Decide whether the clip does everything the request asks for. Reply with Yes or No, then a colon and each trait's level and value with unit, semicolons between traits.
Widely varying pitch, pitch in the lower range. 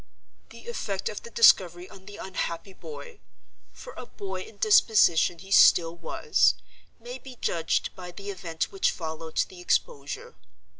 No: wide, 6.6 semitones; high, 190 Hz